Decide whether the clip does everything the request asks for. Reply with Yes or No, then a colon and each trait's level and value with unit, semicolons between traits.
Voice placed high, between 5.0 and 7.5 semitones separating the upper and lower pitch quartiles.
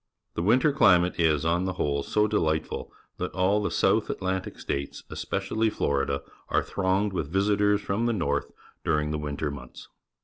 No: very low, 90 Hz; wide, 5.4 semitones